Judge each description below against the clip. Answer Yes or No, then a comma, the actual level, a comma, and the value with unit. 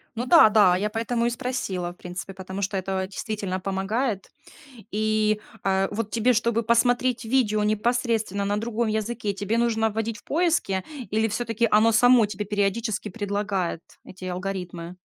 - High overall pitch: Yes, high, 215 Hz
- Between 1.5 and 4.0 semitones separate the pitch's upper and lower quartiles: Yes, average, 3.1 semitones